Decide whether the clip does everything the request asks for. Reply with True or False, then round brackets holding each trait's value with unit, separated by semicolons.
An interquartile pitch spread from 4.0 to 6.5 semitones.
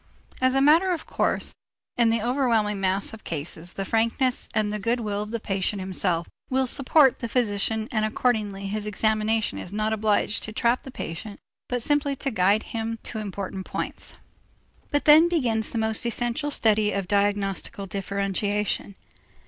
False (3.2 semitones)